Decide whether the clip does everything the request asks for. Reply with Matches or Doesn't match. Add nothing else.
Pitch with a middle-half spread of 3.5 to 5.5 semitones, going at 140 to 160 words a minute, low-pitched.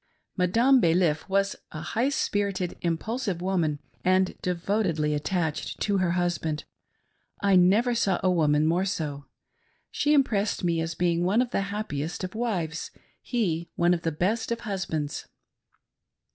Doesn't match